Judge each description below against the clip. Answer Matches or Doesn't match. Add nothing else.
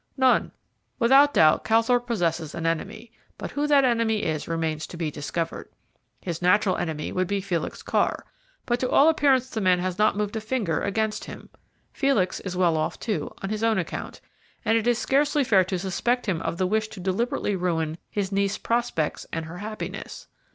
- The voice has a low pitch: Doesn't match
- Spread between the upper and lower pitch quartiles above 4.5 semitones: Matches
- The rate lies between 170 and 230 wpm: Matches